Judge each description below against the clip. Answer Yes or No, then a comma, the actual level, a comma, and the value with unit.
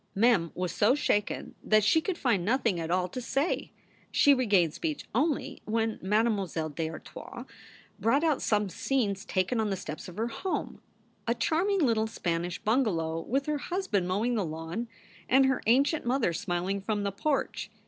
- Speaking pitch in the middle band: No, high, 220 Hz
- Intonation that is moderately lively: No, wide, 6.4 semitones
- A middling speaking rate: Yes, average, 170 wpm